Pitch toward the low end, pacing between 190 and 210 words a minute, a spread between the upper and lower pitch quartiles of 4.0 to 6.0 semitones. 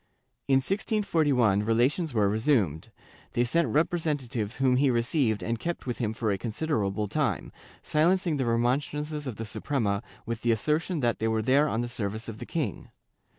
No: low, 120 Hz; average, 175 wpm; average, 5.1 semitones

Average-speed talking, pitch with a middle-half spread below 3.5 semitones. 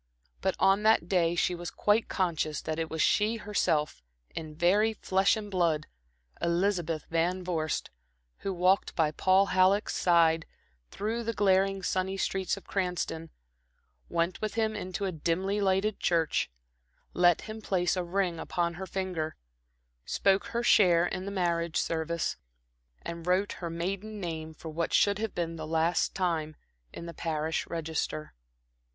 Yes: average, 155 wpm; average, 3.0 semitones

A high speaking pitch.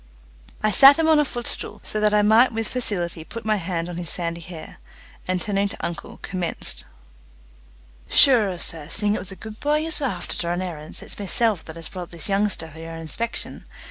Yes: high, 195 Hz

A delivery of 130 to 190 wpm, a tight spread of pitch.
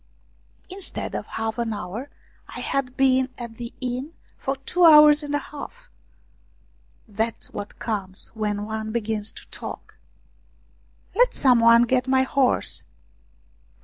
No: average, 140 wpm; average, 4.1 semitones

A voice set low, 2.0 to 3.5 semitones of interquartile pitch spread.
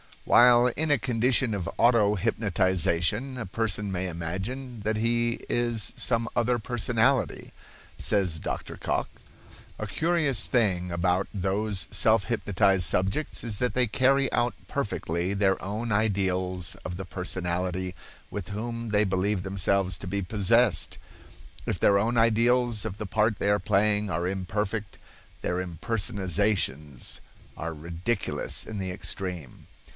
No: low, 100 Hz; average, 4.0 semitones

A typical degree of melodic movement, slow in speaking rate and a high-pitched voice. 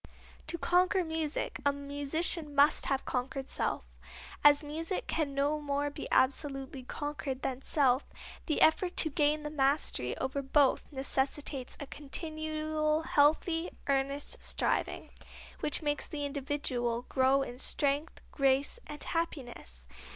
No: narrow, 2.2 semitones; slow, 130 wpm; very high, 290 Hz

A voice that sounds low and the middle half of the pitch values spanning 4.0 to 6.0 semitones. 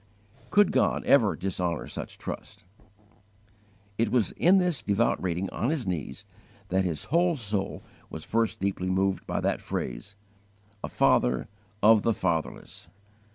Yes: low, 100 Hz; average, 4.3 semitones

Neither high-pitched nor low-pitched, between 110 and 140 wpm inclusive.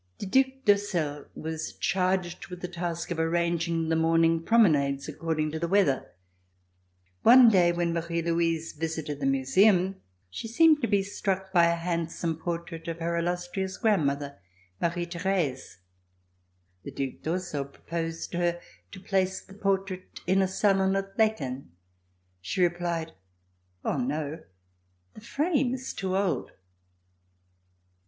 Yes: medium, 170 Hz; slow, 135 wpm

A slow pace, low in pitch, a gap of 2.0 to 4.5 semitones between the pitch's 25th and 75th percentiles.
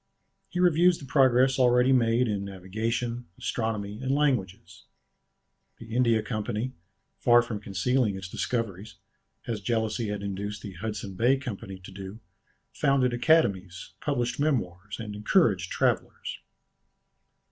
Yes: slow, 125 wpm; low, 110 Hz; average, 4.2 semitones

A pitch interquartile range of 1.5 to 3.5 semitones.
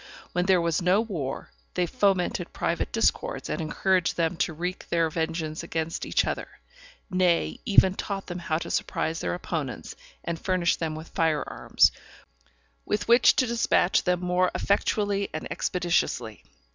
Yes: narrow, 2.6 semitones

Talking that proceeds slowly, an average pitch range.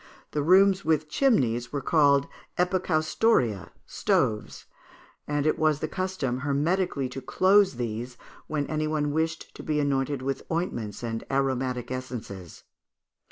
Yes: slow, 130 wpm; average, 4.0 semitones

